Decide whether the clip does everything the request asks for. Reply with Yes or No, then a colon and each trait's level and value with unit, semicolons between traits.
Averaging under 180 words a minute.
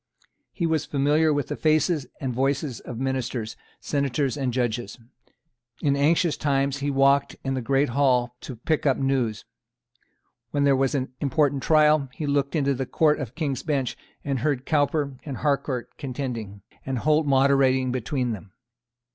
Yes: average, 160 wpm